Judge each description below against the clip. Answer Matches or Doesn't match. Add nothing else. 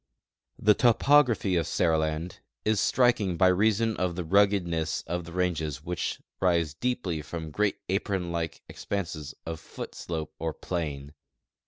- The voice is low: Matches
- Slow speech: Doesn't match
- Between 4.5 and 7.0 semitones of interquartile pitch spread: Doesn't match